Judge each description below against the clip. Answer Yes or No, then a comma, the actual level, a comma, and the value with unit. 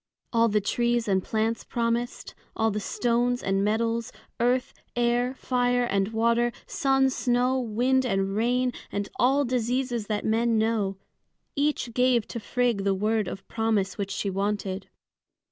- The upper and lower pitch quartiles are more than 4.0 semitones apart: No, average, 2.7 semitones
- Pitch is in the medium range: No, high, 230 Hz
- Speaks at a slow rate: No, average, 145 wpm